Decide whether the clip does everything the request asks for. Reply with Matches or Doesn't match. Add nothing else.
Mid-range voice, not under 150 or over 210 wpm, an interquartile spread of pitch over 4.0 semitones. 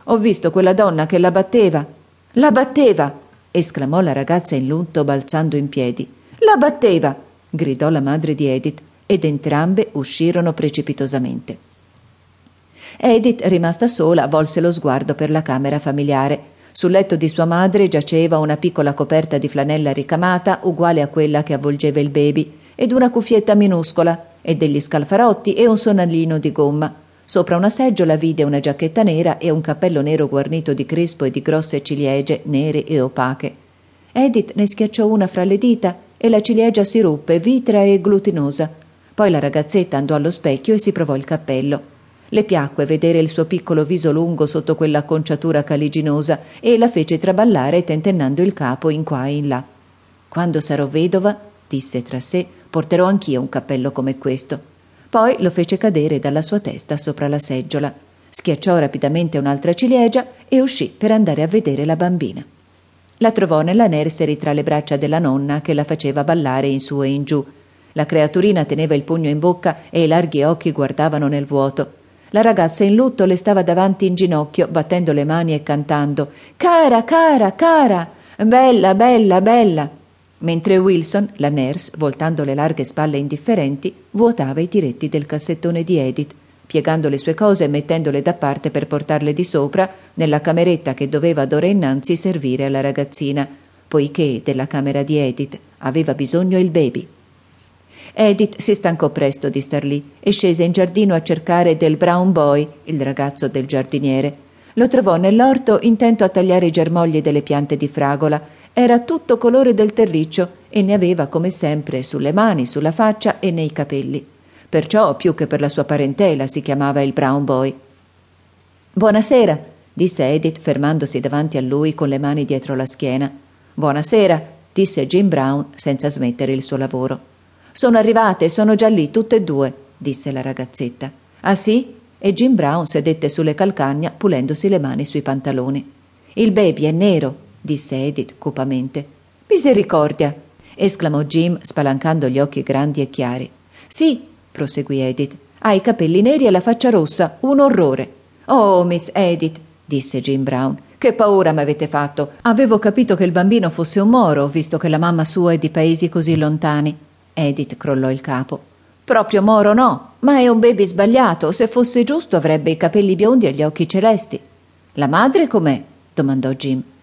Matches